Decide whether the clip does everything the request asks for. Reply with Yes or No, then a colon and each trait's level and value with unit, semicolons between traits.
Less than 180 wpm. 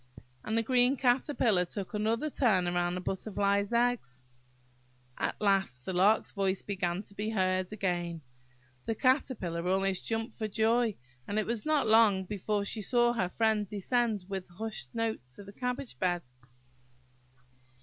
Yes: average, 150 wpm